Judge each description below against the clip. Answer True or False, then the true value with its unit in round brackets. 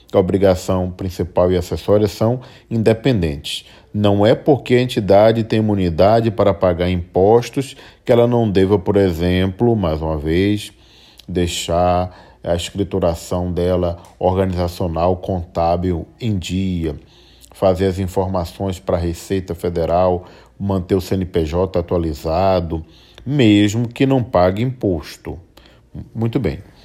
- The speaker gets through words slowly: True (115 wpm)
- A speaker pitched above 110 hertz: False (95 Hz)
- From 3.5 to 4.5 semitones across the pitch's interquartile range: False (3.0 semitones)